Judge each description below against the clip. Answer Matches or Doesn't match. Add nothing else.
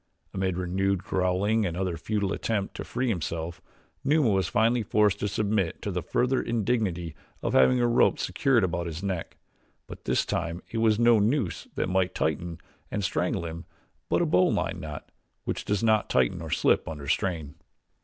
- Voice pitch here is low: Matches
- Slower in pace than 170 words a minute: Doesn't match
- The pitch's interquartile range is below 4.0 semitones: Doesn't match